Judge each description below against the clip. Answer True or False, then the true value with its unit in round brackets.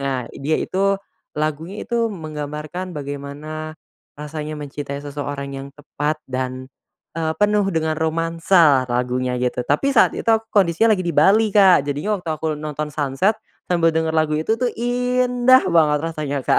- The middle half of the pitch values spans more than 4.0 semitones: True (4.6 semitones)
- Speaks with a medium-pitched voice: True (155 Hz)